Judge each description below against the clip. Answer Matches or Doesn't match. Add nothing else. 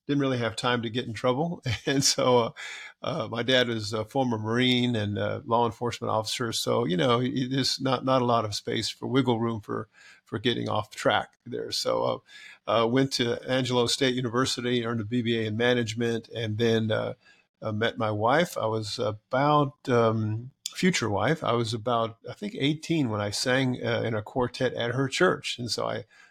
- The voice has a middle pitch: Doesn't match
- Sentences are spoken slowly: Doesn't match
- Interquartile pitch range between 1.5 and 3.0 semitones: Matches